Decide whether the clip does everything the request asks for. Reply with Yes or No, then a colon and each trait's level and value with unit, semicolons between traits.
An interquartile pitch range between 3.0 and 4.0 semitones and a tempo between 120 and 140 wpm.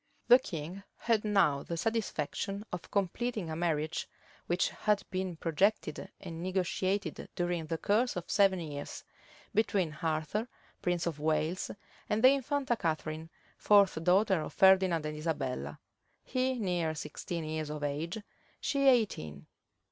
No: average, 4.7 semitones; slow, 135 wpm